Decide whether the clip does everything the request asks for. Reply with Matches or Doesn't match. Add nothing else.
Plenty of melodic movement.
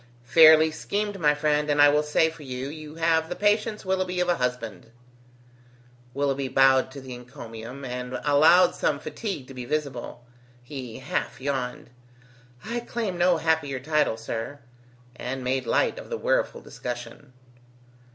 Doesn't match